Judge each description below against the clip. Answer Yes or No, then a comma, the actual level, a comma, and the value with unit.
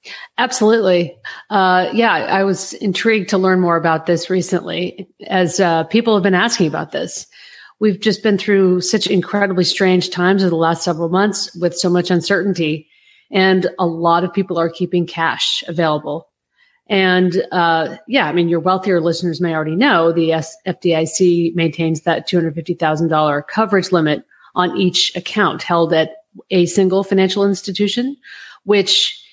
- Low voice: No, medium, 180 Hz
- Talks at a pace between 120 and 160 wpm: Yes, average, 150 wpm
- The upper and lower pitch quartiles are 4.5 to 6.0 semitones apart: No, average, 2.8 semitones